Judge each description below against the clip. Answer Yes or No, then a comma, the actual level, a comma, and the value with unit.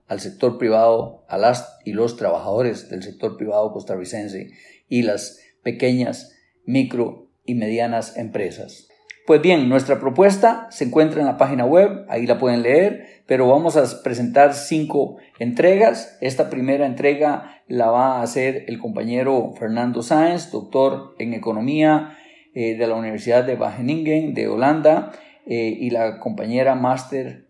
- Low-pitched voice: Yes, low, 130 Hz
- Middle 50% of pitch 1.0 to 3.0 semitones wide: No, average, 4.6 semitones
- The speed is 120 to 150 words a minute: Yes, average, 145 wpm